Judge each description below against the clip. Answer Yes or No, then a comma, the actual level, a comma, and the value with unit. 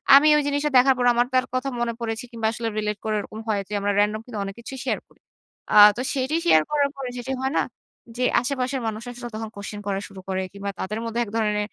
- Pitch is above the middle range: Yes, high, 230 Hz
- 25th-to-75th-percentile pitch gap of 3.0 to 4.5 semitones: Yes, average, 3.5 semitones